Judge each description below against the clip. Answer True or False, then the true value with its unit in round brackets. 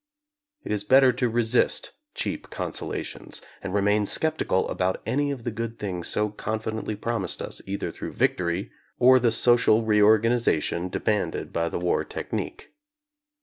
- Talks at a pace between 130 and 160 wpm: True (145 wpm)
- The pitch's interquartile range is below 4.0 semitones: True (3.2 semitones)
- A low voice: True (110 Hz)